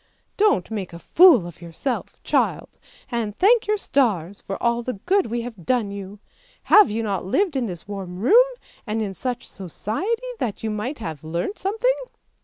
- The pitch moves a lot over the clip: Yes, wide, 6.6 semitones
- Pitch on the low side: No, high, 225 Hz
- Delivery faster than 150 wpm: Yes, average, 180 wpm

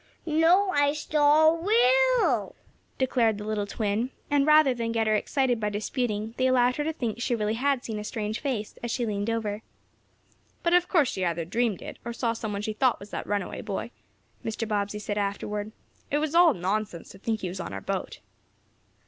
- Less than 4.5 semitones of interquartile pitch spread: No, wide, 5.4 semitones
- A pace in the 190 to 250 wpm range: Yes, average, 200 wpm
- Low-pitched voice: No, high, 230 Hz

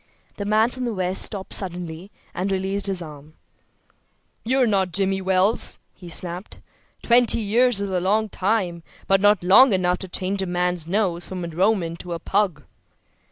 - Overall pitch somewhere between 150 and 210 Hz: Yes, high, 190 Hz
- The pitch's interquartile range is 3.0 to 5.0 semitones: No, narrow, 2.6 semitones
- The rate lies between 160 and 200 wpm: Yes, average, 170 wpm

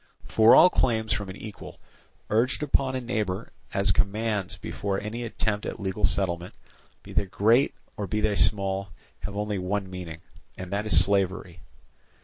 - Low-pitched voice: Yes, low, 100 Hz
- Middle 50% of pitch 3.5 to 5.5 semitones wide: No, narrow, 2.4 semitones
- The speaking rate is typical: Yes, average, 160 wpm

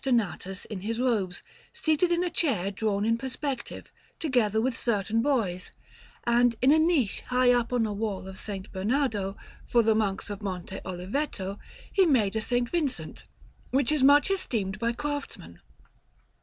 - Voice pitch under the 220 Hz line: No, high, 230 Hz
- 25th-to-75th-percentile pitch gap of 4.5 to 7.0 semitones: Yes, average, 5.1 semitones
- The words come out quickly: No, average, 160 wpm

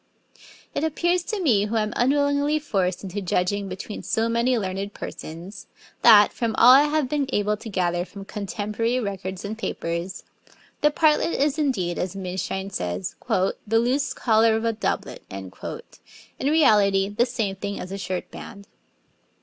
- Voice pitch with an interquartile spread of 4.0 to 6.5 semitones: Yes, average, 4.9 semitones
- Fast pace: No, average, 160 wpm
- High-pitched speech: Yes, high, 210 Hz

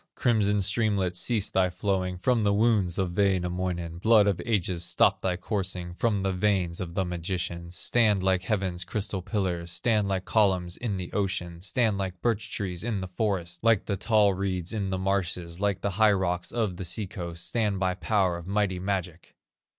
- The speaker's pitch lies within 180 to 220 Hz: No, very low, 95 Hz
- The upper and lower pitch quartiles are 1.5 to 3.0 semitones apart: Yes, narrow, 2.5 semitones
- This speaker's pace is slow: No, average, 185 wpm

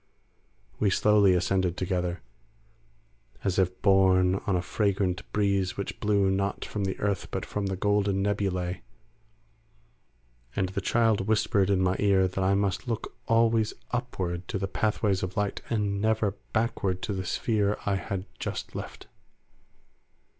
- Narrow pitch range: Yes, narrow, 1.8 semitones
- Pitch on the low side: Yes, low, 100 Hz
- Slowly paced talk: No, average, 145 wpm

